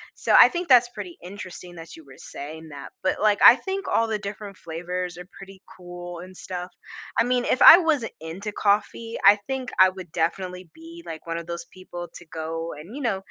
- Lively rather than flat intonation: No, average, 4.6 semitones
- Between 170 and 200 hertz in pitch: Yes, medium, 185 Hz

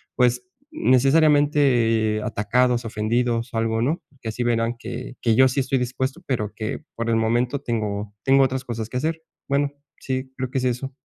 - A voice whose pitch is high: No, low, 125 Hz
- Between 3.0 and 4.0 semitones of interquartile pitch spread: No, narrow, 2.6 semitones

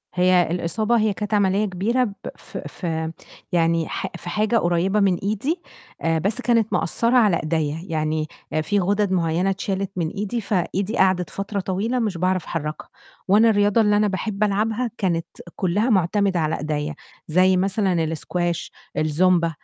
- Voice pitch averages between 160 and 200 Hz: Yes, high, 190 Hz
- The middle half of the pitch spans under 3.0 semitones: No, average, 3.6 semitones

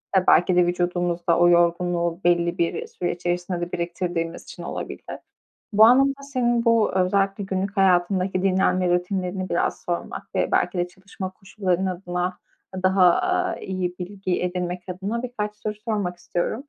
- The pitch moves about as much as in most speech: No, narrow, 2.0 semitones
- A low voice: No, medium, 185 Hz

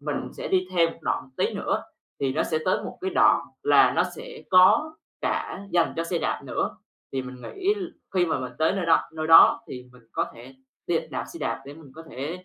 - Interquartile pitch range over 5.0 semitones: Yes, wide, 5.6 semitones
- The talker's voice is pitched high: No, medium, 165 Hz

